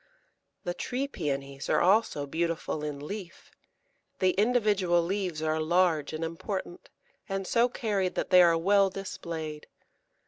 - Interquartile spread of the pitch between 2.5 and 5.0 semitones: Yes, average, 3.8 semitones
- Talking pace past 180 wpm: No, slow, 135 wpm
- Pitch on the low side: No, medium, 175 Hz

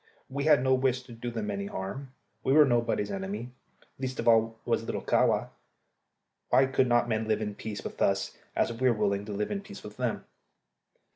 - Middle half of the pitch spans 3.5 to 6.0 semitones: Yes, average, 3.9 semitones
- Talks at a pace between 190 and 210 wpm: Yes, fast, 205 wpm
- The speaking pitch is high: No, low, 115 Hz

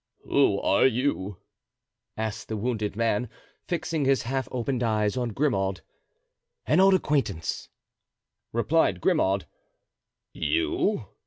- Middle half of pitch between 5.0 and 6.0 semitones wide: Yes, wide, 5.5 semitones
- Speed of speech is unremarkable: No, slow, 105 wpm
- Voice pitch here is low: Yes, low, 125 Hz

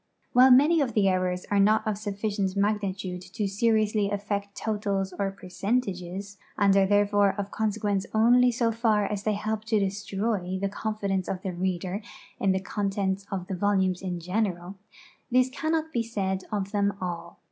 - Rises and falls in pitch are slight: Yes, narrow, 2.2 semitones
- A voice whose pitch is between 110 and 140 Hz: No, high, 200 Hz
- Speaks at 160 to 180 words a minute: Yes, average, 170 wpm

